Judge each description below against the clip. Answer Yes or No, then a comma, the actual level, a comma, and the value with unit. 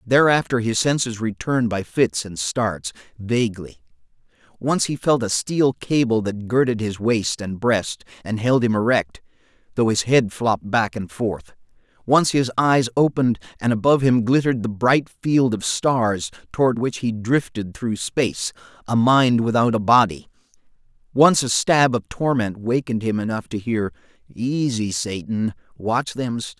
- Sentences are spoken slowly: No, average, 160 wpm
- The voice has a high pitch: No, low, 115 Hz